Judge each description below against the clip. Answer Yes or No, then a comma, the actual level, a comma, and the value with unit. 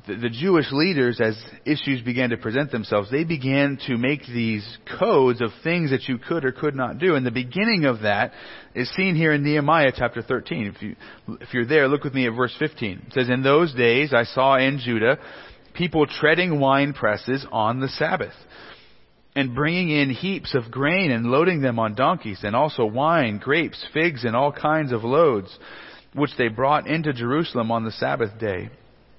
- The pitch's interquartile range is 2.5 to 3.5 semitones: No, average, 4.0 semitones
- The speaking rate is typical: Yes, average, 190 wpm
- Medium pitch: No, low, 130 Hz